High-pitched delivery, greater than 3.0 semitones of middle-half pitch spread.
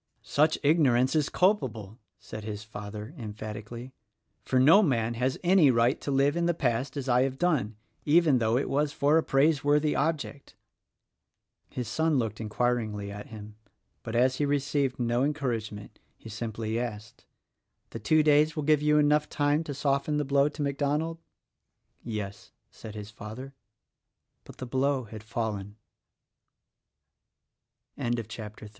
No: low, 130 Hz; average, 4.9 semitones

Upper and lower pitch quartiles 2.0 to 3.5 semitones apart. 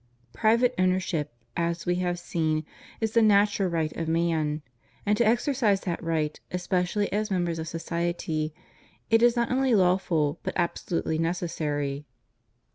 No: average, 4.2 semitones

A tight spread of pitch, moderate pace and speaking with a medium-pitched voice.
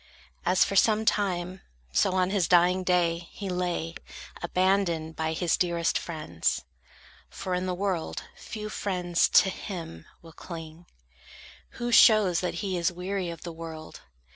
Yes: narrow, 2.2 semitones; average, 145 wpm; medium, 180 Hz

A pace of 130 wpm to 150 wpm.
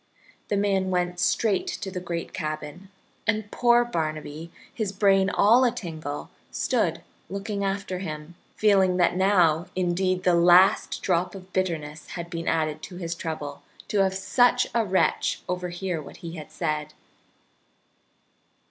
Yes: average, 140 wpm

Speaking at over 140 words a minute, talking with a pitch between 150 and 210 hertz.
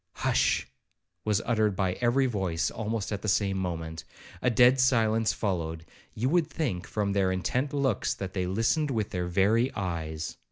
No: average, 160 wpm; low, 105 Hz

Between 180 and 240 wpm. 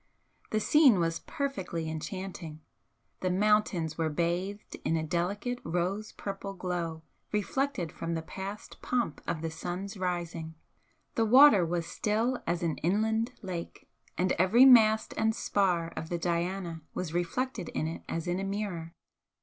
No: average, 150 wpm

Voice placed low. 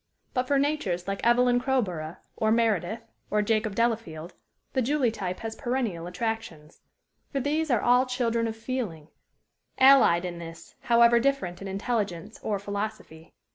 No: high, 225 Hz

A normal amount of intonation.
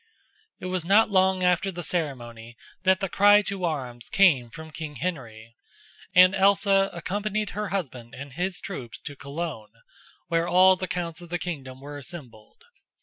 No: wide, 5.7 semitones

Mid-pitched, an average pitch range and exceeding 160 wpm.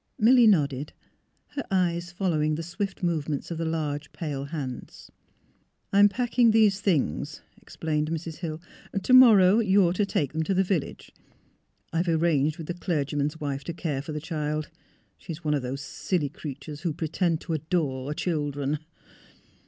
Yes: medium, 160 Hz; average, 3.7 semitones; average, 175 wpm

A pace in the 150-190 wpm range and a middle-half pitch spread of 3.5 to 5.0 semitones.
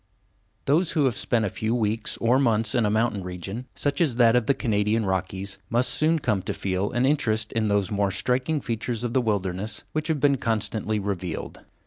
No: fast, 205 wpm; average, 3.8 semitones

